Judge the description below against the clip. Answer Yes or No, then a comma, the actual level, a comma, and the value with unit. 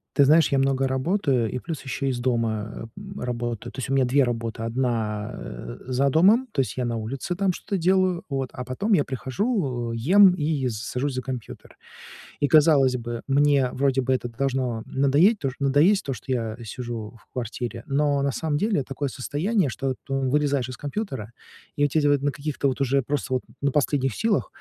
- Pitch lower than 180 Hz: Yes, low, 135 Hz